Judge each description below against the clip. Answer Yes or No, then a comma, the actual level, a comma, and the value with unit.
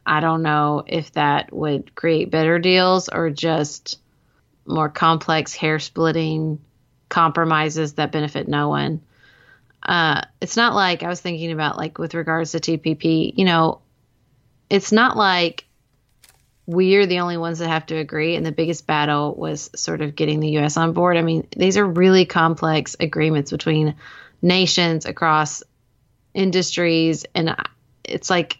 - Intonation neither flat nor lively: No, narrow, 2.0 semitones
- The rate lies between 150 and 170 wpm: Yes, average, 155 wpm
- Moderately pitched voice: Yes, medium, 160 Hz